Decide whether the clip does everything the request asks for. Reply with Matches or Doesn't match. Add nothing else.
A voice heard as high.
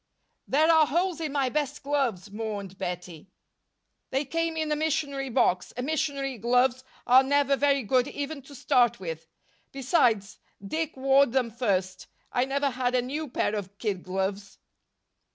Matches